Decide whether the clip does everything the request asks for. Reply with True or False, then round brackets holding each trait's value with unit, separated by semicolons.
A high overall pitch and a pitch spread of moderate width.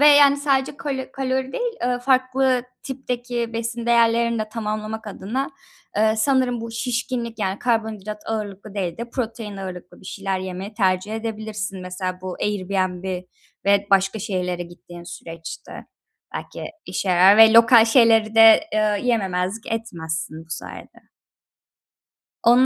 True (220 Hz; 3.9 semitones)